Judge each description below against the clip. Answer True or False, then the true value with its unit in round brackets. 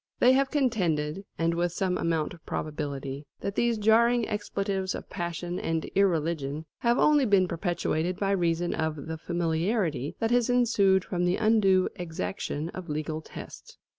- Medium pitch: True (175 Hz)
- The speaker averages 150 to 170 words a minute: True (155 wpm)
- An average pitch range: True (4.5 semitones)